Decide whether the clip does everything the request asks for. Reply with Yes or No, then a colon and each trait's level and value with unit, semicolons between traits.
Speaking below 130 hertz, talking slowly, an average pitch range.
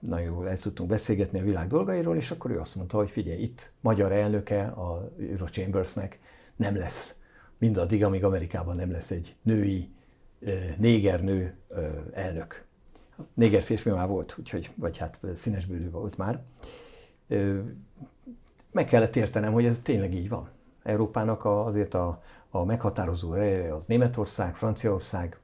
No: low, 100 Hz; average, 140 wpm; average, 3.2 semitones